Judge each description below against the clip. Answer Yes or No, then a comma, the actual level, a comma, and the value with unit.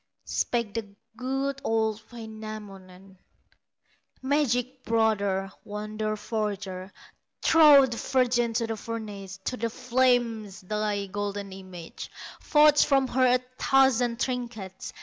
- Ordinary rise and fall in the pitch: Yes, average, 3.6 semitones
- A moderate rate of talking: No, slow, 110 wpm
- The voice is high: Yes, high, 225 Hz